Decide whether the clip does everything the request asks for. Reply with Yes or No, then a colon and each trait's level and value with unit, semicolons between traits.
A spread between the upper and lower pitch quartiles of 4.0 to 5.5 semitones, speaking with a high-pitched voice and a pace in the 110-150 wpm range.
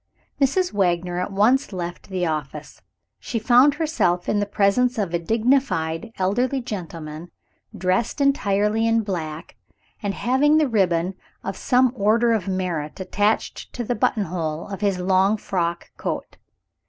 Yes: average, 5.1 semitones; high, 200 Hz; average, 140 wpm